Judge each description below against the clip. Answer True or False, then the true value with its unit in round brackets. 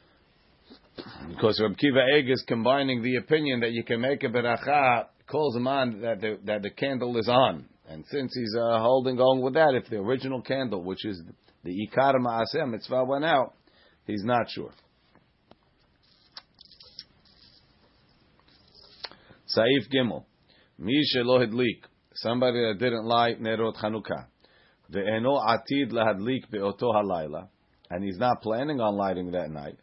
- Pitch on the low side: True (120 Hz)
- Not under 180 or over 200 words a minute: False (135 wpm)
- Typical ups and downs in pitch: True (3.4 semitones)